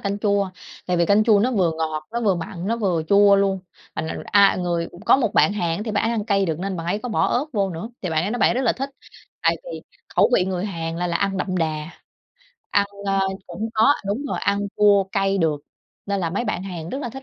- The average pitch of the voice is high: Yes, high, 195 Hz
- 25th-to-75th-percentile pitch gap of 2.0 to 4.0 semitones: Yes, average, 3.4 semitones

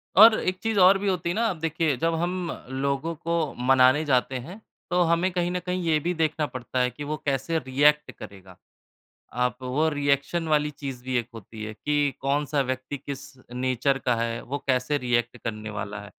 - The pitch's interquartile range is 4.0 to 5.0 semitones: Yes, average, 4.6 semitones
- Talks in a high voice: No, medium, 140 Hz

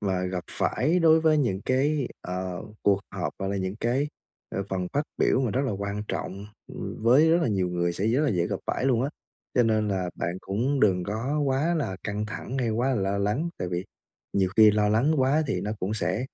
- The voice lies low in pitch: Yes, low, 110 Hz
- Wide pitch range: Yes, wide, 5.8 semitones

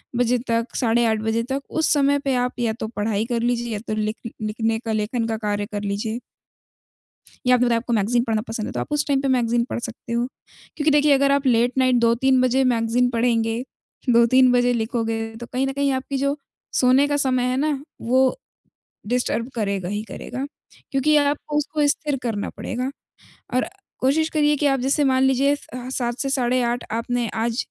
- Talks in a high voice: Yes, high, 245 Hz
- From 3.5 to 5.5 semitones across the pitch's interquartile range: No, average, 2.9 semitones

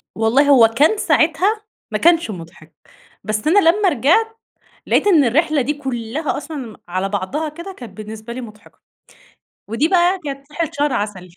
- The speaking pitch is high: Yes, very high, 280 Hz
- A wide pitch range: Yes, wide, 6.9 semitones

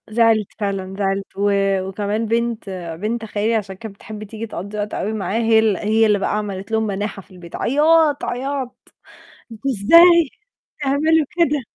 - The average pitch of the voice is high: Yes, high, 220 Hz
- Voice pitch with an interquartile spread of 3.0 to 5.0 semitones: Yes, average, 3.5 semitones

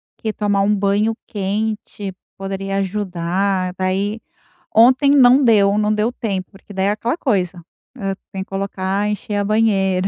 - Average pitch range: No, narrow, 1.8 semitones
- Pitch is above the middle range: Yes, high, 200 Hz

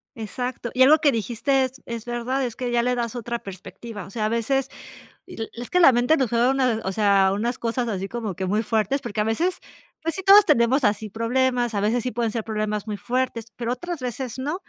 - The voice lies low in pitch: No, high, 235 Hz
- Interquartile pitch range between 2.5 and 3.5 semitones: Yes, average, 3.1 semitones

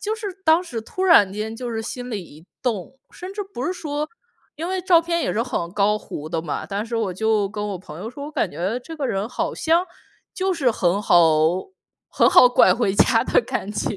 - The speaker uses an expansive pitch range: Yes, wide, 8.6 semitones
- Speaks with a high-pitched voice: Yes, high, 230 Hz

